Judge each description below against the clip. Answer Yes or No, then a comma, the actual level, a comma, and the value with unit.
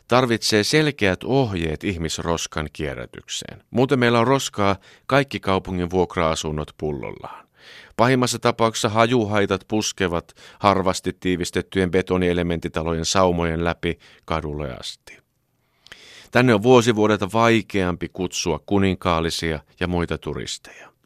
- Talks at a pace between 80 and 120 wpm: Yes, slow, 95 wpm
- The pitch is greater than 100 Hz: No, very low, 95 Hz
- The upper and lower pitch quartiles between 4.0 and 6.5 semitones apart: Yes, average, 5.2 semitones